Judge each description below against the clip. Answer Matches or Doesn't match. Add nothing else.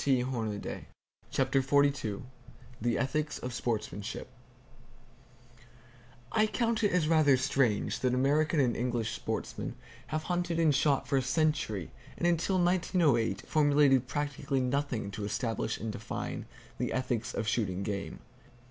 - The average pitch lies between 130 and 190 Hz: Matches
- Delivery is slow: Matches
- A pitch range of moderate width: Matches